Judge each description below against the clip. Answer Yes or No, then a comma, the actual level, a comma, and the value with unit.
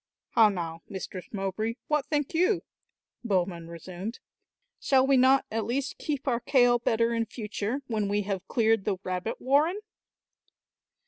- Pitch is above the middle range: Yes, high, 225 Hz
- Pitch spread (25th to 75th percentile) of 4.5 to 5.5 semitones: Yes, average, 5.2 semitones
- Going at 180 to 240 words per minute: No, average, 145 wpm